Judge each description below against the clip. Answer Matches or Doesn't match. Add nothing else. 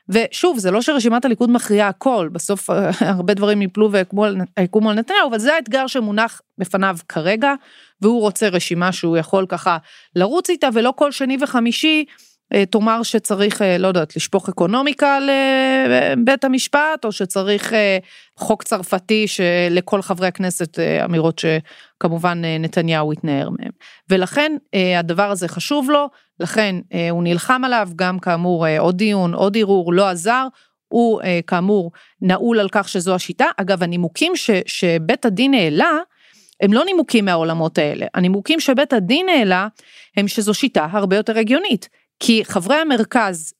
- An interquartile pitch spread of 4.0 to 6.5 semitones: Matches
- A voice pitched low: Doesn't match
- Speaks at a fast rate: Doesn't match